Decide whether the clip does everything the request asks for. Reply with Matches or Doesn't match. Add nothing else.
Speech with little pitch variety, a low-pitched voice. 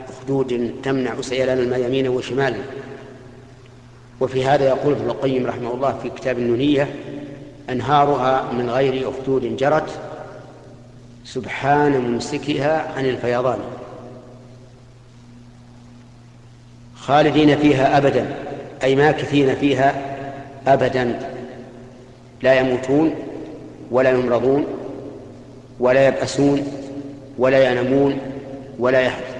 Matches